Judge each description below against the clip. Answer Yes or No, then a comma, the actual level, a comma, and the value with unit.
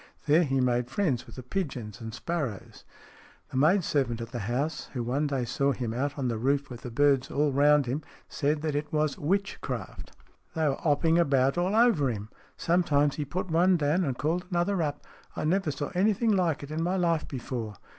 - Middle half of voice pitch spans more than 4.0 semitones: Yes, average, 4.6 semitones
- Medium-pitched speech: Yes, medium, 145 Hz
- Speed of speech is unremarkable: No, fast, 210 wpm